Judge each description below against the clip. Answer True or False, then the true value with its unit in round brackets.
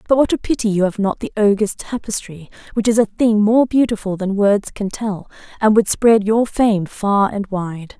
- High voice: True (210 Hz)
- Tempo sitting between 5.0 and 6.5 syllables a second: False (4.7 syllables/s)